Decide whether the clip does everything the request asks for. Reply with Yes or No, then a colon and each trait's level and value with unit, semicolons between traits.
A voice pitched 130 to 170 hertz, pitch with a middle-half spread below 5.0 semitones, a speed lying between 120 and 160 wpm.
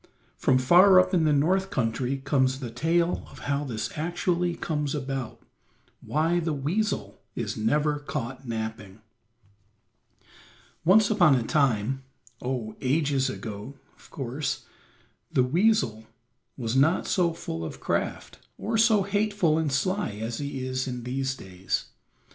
No: medium, 140 Hz; wide, 5.4 semitones; slow, 135 wpm